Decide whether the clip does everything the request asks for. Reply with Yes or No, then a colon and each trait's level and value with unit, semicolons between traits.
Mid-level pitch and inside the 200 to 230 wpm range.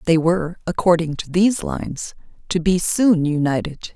No: medium, 170 Hz; average, 150 wpm